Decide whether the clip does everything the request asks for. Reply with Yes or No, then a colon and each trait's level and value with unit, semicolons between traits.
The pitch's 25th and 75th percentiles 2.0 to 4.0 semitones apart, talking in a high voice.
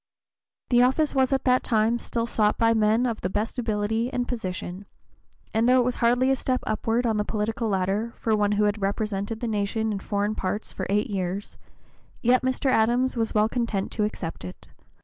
Yes: average, 2.8 semitones; high, 220 Hz